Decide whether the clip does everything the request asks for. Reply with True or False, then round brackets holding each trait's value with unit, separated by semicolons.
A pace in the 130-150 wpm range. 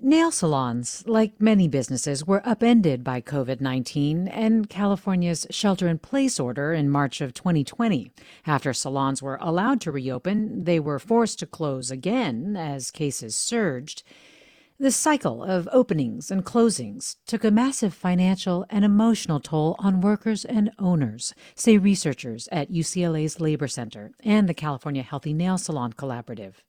True (140 wpm)